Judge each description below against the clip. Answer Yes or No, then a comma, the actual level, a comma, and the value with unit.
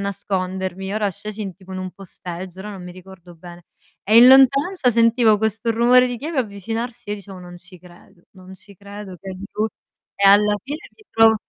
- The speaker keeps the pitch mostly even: No, average, 3.3 semitones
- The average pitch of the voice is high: Yes, high, 200 Hz